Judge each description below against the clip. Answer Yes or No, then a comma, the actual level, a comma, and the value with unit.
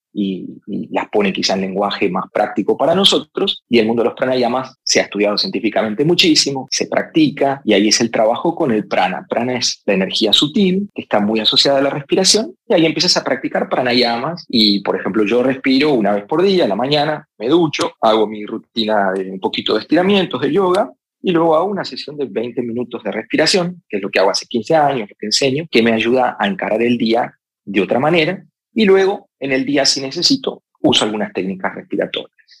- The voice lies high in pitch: No, low, 130 Hz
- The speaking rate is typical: No, fast, 215 wpm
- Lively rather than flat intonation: Yes, wide, 7.5 semitones